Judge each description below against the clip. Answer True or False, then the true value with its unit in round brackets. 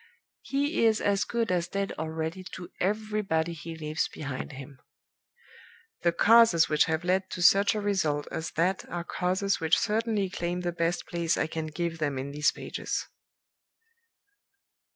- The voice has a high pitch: False (175 Hz)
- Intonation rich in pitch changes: False (3.7 semitones)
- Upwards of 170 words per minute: False (155 wpm)